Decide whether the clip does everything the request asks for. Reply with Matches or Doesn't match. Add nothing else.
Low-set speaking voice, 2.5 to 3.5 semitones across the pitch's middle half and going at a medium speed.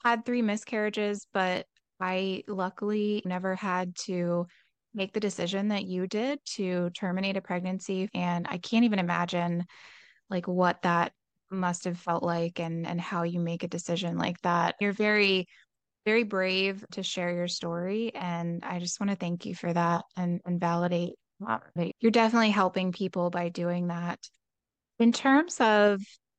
Doesn't match